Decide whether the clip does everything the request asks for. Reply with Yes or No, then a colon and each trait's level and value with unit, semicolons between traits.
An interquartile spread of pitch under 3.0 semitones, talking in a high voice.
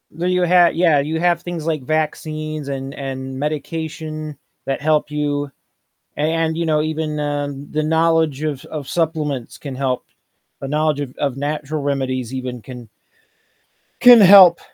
No: narrow, 2.5 semitones; medium, 150 Hz